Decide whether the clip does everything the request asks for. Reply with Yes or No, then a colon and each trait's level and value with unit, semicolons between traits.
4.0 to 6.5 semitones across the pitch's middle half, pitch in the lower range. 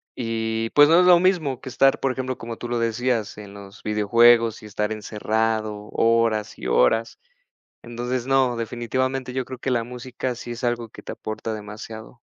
No: average, 2.7 semitones; low, 115 Hz